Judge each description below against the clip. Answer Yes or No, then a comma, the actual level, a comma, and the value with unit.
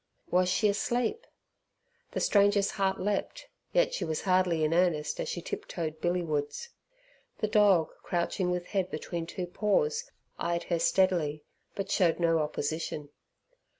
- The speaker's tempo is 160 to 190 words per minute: No, average, 150 wpm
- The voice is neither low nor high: Yes, medium, 180 Hz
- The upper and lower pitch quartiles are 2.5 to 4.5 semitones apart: Yes, average, 3.5 semitones